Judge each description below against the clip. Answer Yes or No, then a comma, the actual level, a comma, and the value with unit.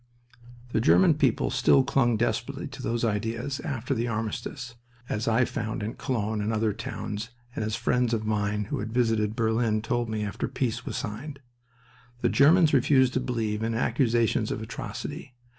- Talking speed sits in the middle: Yes, average, 170 wpm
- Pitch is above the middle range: No, low, 115 Hz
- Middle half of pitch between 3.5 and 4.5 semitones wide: No, narrow, 2.6 semitones